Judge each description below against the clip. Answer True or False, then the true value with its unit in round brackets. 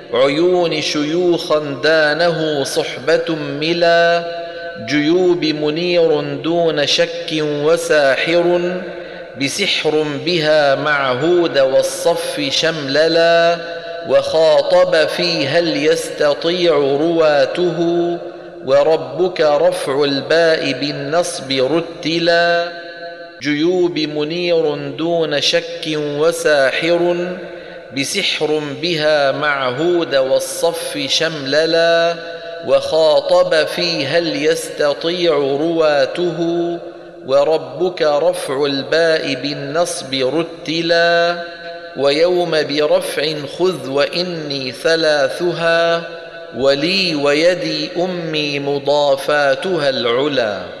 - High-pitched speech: False (165 Hz)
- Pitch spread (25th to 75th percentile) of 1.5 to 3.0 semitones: True (2.4 semitones)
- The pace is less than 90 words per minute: True (65 wpm)